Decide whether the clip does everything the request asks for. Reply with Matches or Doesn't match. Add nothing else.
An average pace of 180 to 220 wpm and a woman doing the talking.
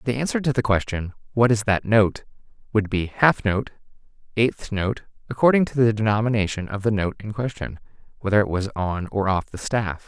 Doesn't match